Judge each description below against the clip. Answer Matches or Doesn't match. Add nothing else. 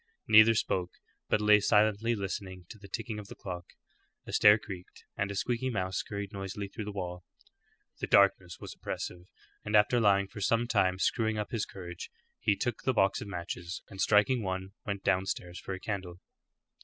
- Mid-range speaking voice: Doesn't match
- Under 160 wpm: Doesn't match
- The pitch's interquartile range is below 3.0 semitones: Matches